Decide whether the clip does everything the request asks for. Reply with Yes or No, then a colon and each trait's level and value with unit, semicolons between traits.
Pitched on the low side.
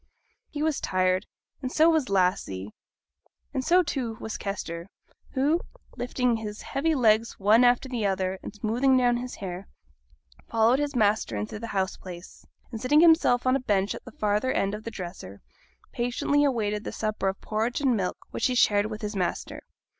No: high, 220 Hz